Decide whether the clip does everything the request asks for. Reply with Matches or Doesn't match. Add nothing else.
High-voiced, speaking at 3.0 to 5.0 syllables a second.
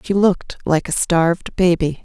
Doesn't match